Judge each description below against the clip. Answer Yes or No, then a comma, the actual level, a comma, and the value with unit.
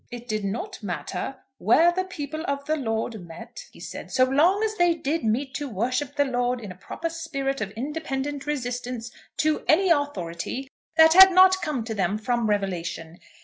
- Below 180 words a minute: No, average, 185 wpm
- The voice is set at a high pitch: Yes, very high, 265 Hz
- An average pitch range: No, wide, 5.8 semitones